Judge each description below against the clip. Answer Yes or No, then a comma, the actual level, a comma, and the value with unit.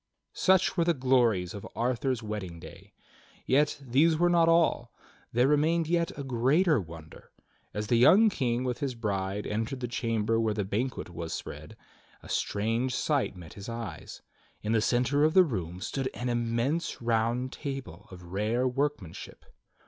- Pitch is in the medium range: No, low, 120 Hz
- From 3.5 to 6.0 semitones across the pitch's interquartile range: Yes, average, 5.0 semitones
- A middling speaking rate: Yes, average, 165 wpm